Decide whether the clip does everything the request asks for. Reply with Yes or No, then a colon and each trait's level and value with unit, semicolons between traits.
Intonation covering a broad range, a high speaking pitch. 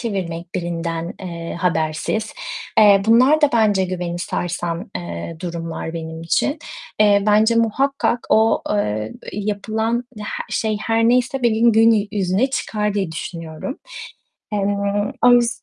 No: average, 4.9 semitones; high, 205 Hz